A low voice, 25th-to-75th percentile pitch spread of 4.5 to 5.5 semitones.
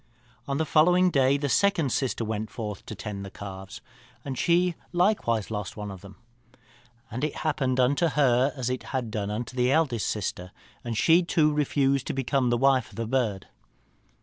Yes: low, 130 Hz; average, 5.1 semitones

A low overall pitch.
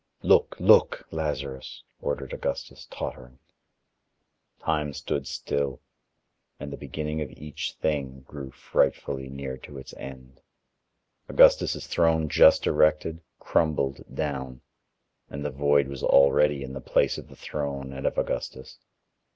Yes: very low, 70 Hz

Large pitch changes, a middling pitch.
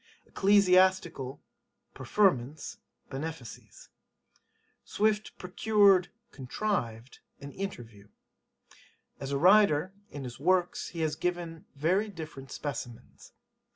Yes: wide, 5.9 semitones; medium, 165 Hz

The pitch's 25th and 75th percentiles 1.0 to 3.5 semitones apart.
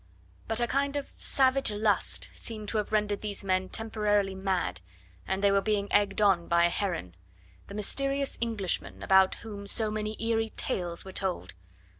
Yes: narrow, 2.6 semitones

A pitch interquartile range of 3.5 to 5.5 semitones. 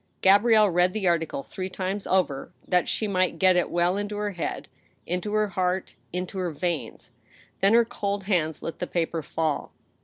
No: average, 2.7 semitones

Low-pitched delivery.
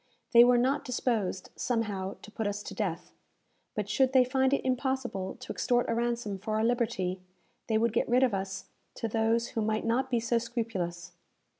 No: high, 230 Hz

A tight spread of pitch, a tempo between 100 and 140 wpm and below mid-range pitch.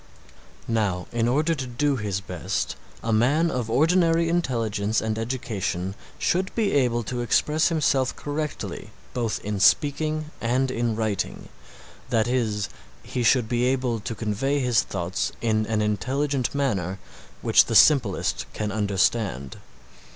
No: average, 4.8 semitones; slow, 135 wpm; low, 120 Hz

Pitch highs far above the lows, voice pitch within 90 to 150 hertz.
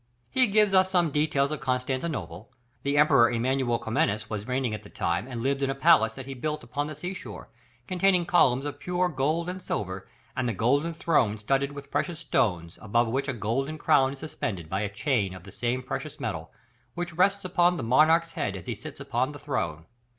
Yes: wide, 5.7 semitones; low, 135 Hz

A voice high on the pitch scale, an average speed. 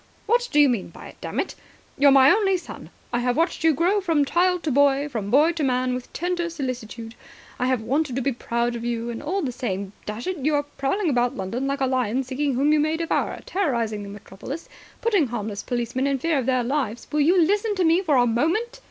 No: very high, 275 Hz; fast, 240 wpm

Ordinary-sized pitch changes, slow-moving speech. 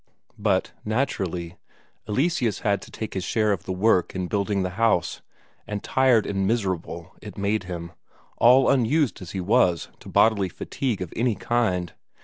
No: average, 4.0 semitones; average, 160 wpm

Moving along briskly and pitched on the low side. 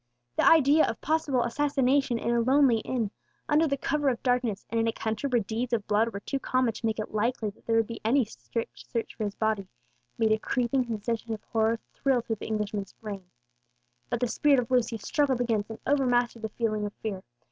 No: fast, 215 wpm; high, 230 Hz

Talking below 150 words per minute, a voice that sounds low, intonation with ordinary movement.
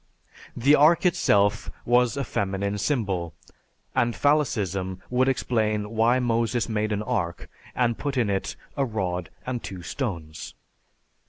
Yes: average, 140 wpm; low, 110 Hz; average, 4.2 semitones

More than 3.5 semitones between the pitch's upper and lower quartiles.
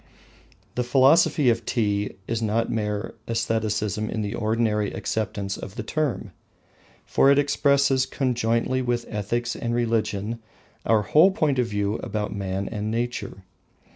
No: average, 2.8 semitones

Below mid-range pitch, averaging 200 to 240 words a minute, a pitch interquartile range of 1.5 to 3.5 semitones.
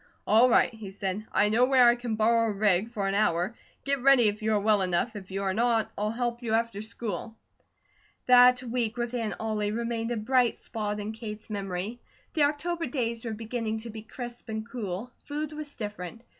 No: high, 225 Hz; fast, 205 wpm; narrow, 2.6 semitones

